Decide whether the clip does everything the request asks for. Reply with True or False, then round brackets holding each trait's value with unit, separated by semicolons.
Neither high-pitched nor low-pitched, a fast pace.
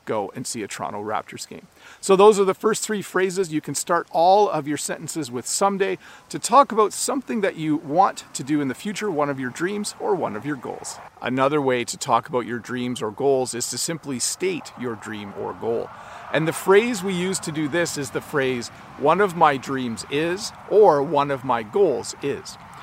True (155 Hz; 220 wpm)